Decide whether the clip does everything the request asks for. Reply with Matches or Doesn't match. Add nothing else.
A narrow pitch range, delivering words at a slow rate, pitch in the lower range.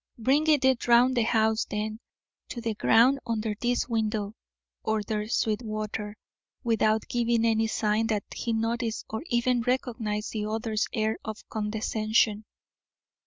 Doesn't match